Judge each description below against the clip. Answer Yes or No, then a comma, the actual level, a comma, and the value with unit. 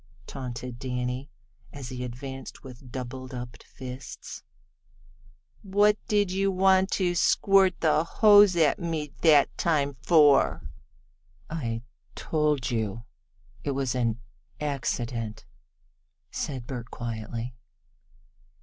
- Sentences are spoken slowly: Yes, slow, 100 wpm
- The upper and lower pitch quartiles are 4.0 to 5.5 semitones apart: Yes, average, 5.2 semitones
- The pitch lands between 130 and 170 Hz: Yes, low, 135 Hz